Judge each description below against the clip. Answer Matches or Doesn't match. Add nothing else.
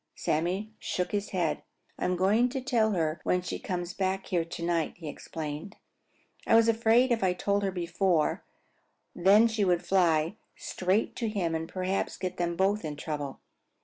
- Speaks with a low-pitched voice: Doesn't match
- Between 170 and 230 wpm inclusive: Matches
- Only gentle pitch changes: Doesn't match